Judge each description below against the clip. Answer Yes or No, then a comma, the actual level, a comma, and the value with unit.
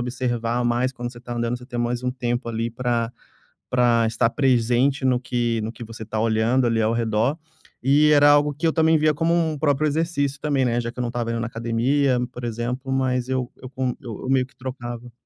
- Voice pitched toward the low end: Yes, low, 125 Hz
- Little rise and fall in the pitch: Yes, narrow, 2.3 semitones